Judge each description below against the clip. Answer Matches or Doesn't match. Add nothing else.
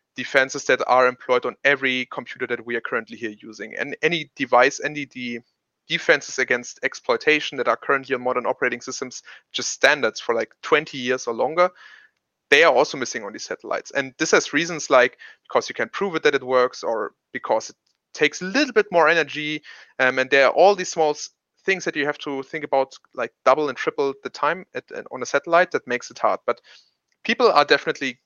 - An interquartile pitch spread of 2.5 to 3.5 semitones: Doesn't match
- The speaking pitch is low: Doesn't match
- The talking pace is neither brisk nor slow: Doesn't match